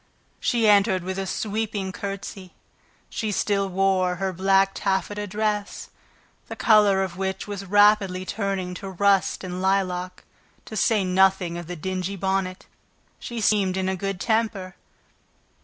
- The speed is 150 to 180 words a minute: No, average, 140 wpm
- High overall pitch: Yes, high, 195 Hz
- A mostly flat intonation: Yes, narrow, 1.7 semitones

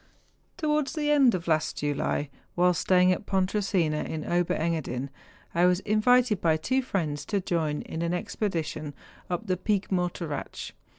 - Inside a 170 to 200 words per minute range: No, average, 160 wpm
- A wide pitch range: No, average, 4.6 semitones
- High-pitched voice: No, medium, 180 Hz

